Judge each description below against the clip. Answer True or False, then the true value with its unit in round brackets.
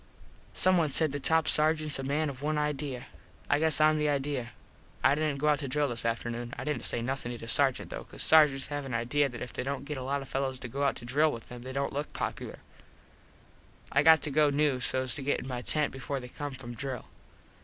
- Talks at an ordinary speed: False (245 wpm)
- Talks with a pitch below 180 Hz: True (140 Hz)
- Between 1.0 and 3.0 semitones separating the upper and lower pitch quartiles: True (2.7 semitones)